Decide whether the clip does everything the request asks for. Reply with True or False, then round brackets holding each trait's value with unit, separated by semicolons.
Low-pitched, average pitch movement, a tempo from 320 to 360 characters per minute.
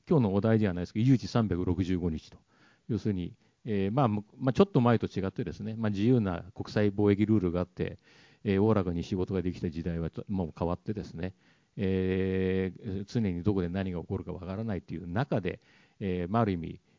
False (100 Hz; 3.6 semitones; 385 characters per minute)